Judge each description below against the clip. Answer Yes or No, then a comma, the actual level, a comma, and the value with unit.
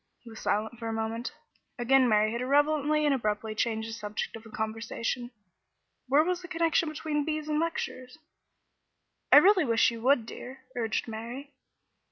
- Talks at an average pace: Yes, average, 165 wpm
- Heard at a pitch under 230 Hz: No, high, 245 Hz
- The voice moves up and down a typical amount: Yes, average, 5.0 semitones